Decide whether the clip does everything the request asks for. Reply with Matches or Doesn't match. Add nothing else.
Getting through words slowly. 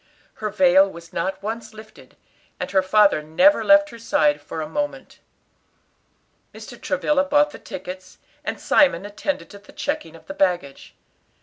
Doesn't match